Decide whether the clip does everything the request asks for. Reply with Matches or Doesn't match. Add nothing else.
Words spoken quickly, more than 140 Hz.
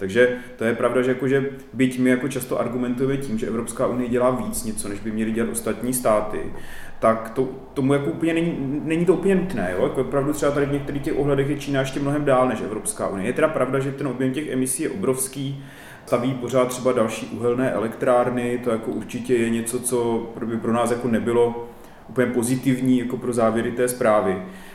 Doesn't match